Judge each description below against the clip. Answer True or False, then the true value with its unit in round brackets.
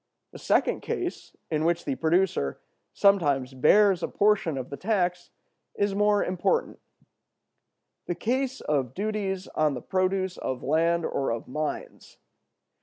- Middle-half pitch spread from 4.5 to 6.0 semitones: True (5.1 semitones)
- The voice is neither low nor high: True (175 Hz)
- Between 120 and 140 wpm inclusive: True (135 wpm)